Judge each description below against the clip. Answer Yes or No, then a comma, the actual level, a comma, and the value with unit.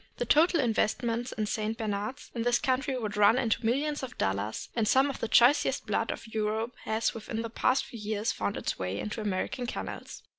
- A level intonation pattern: No, average, 3.0 semitones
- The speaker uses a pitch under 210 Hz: No, high, 230 Hz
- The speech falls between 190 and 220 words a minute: Yes, average, 200 wpm